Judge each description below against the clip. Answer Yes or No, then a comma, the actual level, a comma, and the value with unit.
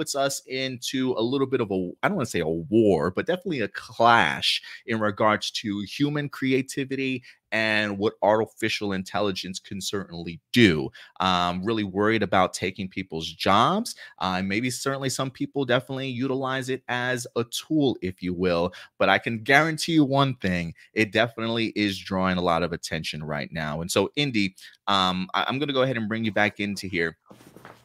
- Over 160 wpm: Yes, average, 185 wpm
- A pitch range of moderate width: No, wide, 5.8 semitones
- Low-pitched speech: Yes, low, 110 Hz